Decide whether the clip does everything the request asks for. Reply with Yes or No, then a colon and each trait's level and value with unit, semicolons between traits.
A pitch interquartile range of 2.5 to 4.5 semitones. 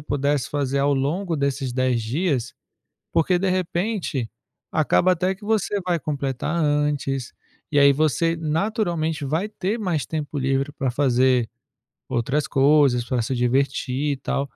Yes: average, 3.9 semitones